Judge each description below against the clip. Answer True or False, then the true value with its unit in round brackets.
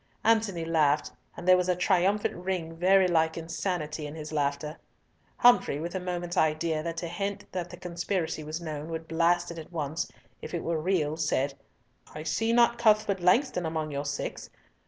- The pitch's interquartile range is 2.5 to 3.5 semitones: True (2.8 semitones)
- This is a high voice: False (170 Hz)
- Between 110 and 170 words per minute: False (180 wpm)